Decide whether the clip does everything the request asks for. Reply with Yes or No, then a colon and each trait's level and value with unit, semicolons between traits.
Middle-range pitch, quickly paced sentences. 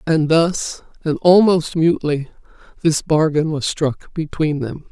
No: medium, 155 Hz; slow, 135 wpm